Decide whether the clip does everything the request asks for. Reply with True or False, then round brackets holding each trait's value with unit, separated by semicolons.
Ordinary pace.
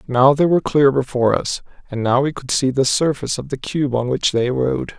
False (240 wpm)